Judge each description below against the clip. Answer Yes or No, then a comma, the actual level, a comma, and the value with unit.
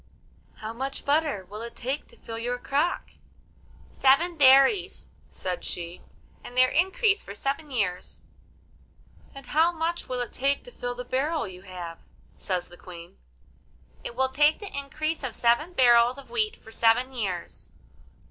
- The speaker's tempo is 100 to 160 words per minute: Yes, average, 155 wpm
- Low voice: No, very high, 260 Hz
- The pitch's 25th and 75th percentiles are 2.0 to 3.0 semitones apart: No, average, 5.2 semitones